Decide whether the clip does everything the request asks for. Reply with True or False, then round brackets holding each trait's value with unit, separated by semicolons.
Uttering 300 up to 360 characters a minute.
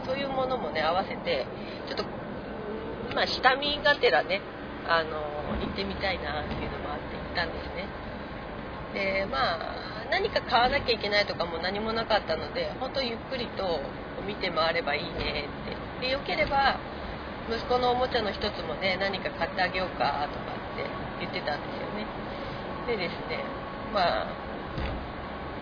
True (325 characters per minute)